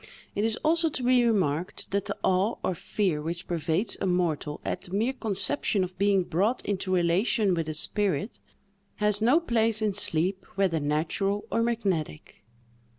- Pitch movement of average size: Yes, average, 4.3 semitones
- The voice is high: Yes, high, 195 Hz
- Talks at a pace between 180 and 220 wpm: No, average, 165 wpm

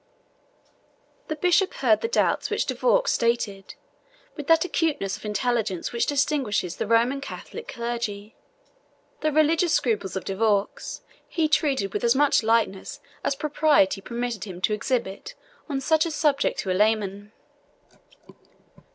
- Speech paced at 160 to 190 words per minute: No, average, 145 wpm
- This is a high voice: Yes, high, 235 Hz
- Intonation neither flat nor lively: No, wide, 6.5 semitones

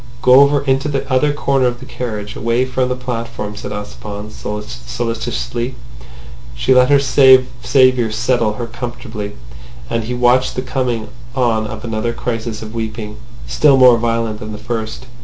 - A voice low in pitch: Yes, low, 120 Hz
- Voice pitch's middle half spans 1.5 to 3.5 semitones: Yes, narrow, 2.6 semitones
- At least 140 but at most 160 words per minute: Yes, average, 155 wpm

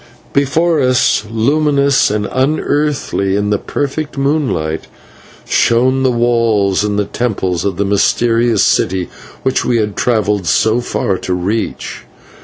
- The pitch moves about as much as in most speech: Yes, average, 4.8 semitones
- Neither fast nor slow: No, slow, 125 wpm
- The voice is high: No, low, 115 Hz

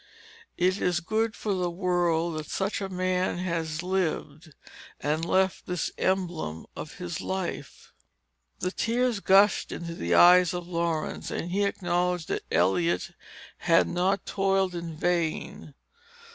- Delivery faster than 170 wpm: No, slow, 135 wpm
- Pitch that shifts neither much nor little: No, narrow, 2.2 semitones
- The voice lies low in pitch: No, medium, 180 Hz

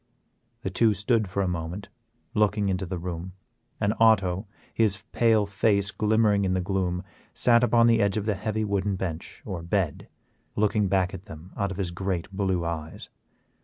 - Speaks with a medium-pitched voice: No, low, 100 Hz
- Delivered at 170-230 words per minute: Yes, average, 175 wpm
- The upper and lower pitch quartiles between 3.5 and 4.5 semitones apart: No, narrow, 2.6 semitones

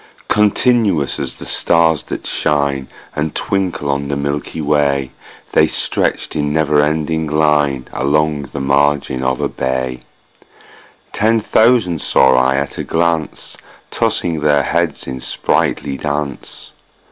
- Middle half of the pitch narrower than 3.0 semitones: Yes, narrow, 2.6 semitones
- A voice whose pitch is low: Yes, very low, 75 Hz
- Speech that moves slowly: Yes, slow, 130 wpm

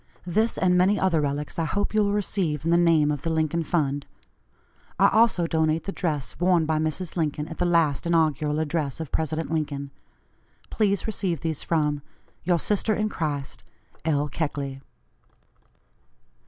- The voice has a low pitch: No, medium, 160 Hz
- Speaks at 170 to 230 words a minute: No, average, 160 wpm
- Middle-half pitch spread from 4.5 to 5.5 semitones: No, average, 3.1 semitones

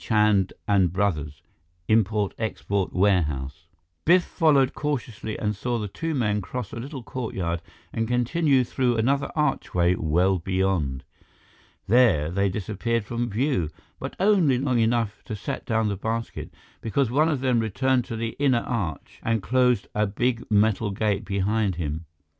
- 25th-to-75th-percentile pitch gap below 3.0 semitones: No, average, 4.5 semitones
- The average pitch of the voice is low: Yes, low, 110 Hz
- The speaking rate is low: No, average, 150 wpm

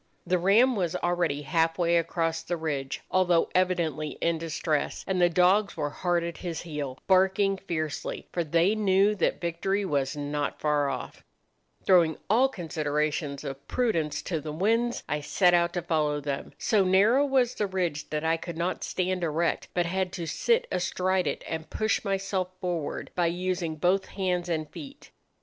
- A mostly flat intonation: No, average, 3.4 semitones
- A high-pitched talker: No, medium, 175 Hz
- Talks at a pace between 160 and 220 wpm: Yes, average, 170 wpm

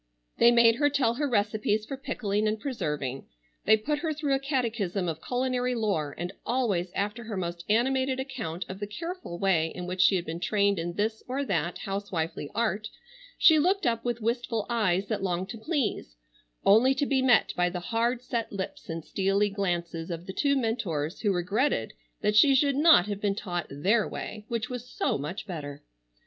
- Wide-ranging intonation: Yes, wide, 5.7 semitones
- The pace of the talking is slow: No, average, 190 wpm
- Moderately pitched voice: No, high, 210 Hz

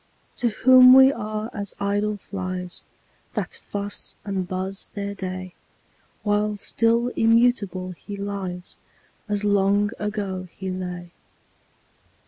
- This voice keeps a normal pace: No, slow, 110 wpm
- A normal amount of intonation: No, narrow, 2.3 semitones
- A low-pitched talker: No, high, 200 Hz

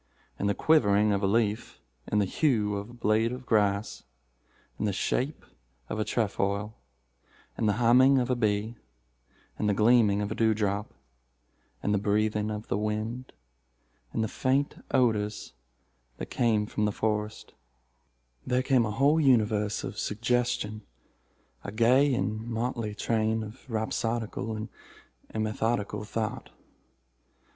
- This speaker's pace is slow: Yes, slow, 125 wpm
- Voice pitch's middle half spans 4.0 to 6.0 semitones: No, narrow, 2.5 semitones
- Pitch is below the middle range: Yes, low, 105 Hz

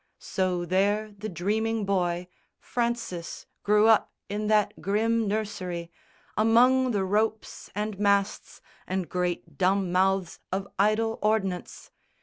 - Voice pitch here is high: Yes, high, 200 Hz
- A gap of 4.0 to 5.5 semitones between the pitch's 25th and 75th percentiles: No, average, 2.7 semitones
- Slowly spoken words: Yes, slow, 120 wpm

